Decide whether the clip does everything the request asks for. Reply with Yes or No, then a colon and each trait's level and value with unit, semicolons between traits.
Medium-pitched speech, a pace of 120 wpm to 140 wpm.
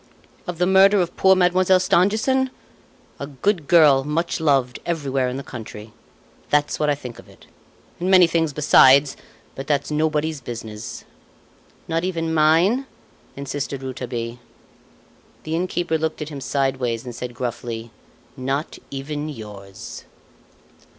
Yes: medium, 150 Hz; slow, 135 wpm